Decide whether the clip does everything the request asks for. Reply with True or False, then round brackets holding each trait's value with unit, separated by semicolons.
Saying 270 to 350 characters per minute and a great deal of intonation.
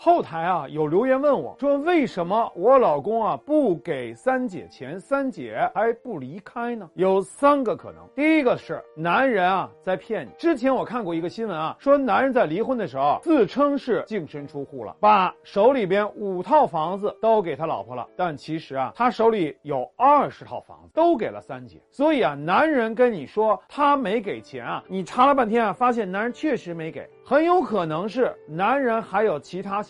True (280 characters per minute; 6.7 semitones)